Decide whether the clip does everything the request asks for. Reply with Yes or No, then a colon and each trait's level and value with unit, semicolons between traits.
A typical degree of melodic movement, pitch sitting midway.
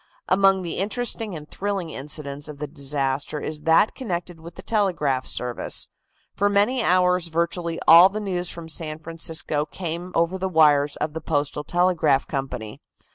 Yes: average, 3.7 semitones; medium, 165 Hz